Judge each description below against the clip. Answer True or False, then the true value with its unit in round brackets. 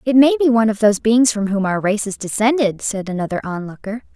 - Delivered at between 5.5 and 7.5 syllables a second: True (6.0 syllables/s)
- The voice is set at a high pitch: True (220 Hz)